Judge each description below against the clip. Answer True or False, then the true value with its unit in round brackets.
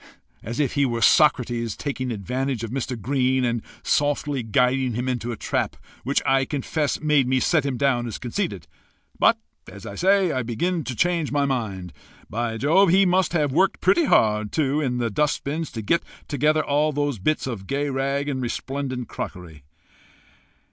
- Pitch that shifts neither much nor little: True (3.8 semitones)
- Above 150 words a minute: True (180 wpm)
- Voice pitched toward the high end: False (135 Hz)